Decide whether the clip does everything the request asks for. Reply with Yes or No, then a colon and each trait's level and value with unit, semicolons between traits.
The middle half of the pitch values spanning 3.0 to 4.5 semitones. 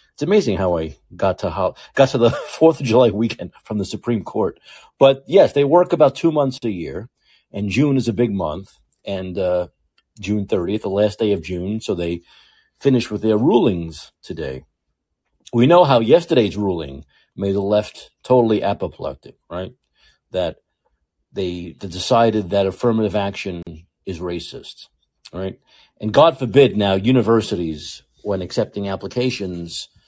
No: average, 5.3 semitones